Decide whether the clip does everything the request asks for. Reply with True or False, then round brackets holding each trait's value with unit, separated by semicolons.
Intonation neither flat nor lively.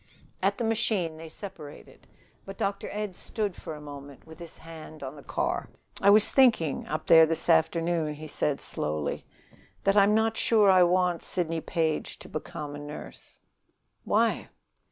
True (4.4 semitones)